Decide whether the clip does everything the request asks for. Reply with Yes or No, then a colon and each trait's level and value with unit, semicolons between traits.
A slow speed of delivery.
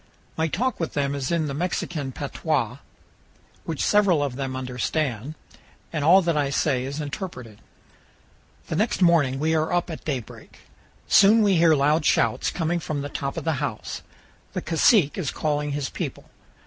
No: average, 170 wpm